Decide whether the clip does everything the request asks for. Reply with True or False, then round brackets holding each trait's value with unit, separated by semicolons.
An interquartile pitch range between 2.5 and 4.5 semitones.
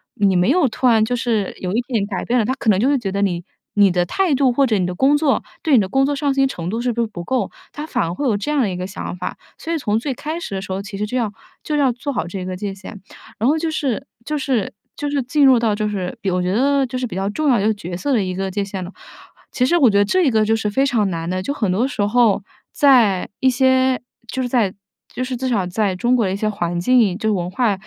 False (5.3 semitones)